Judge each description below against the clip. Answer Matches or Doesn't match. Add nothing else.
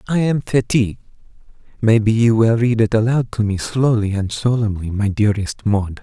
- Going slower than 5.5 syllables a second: Matches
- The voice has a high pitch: Doesn't match